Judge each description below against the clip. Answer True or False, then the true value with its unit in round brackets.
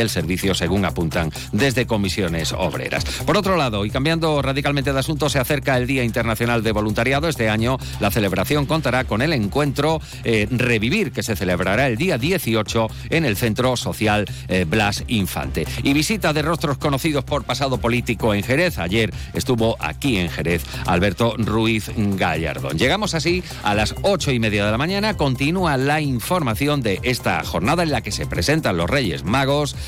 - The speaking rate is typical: True (175 wpm)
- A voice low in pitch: True (125 Hz)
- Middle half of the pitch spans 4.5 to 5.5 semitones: True (5.2 semitones)